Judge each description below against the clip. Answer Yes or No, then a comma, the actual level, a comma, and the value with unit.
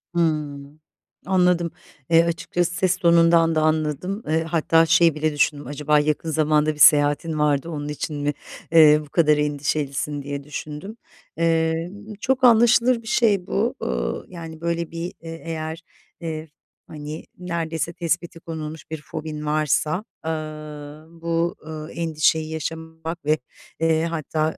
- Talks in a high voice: No, medium, 160 Hz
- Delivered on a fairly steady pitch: Yes, narrow, 1.8 semitones